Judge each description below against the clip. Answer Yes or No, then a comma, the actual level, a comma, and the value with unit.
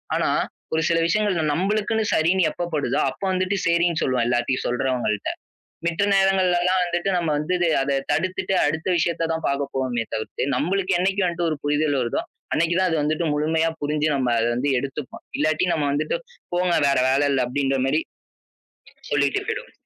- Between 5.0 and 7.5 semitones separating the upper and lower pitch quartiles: No, average, 4.2 semitones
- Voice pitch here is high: No, medium, 155 Hz